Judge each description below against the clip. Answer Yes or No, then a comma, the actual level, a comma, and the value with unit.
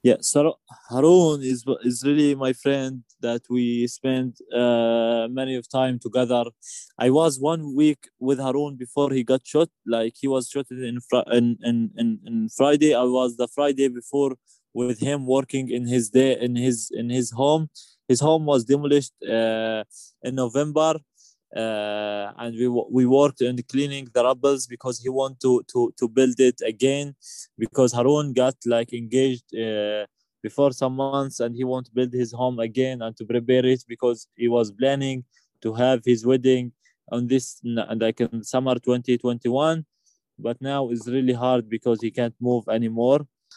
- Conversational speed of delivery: Yes, average, 170 wpm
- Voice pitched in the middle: No, low, 125 Hz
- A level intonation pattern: Yes, narrow, 2.3 semitones